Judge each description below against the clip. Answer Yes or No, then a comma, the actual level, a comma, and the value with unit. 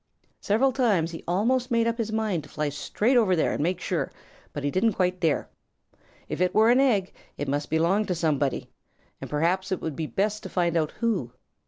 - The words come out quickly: Yes, fast, 210 wpm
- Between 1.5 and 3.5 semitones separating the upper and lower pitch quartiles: No, wide, 5.5 semitones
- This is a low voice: No, medium, 185 Hz